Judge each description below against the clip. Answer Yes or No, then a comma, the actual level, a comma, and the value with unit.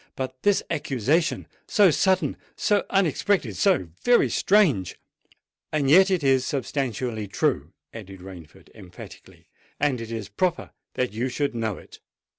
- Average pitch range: No, wide, 8.2 semitones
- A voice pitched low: Yes, low, 130 Hz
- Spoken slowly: Yes, slow, 120 wpm